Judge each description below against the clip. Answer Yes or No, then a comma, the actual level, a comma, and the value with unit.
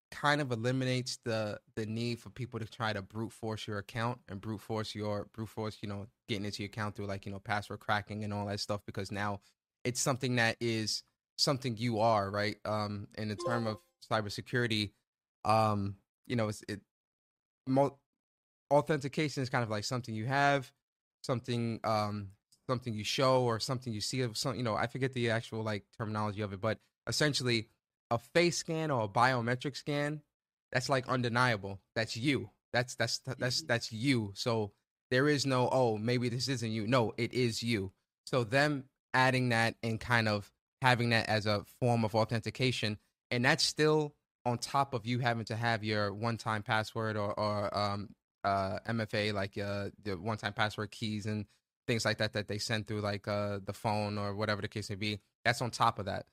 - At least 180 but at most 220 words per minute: Yes, average, 195 wpm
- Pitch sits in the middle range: No, low, 115 Hz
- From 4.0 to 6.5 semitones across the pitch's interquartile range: No, average, 3.1 semitones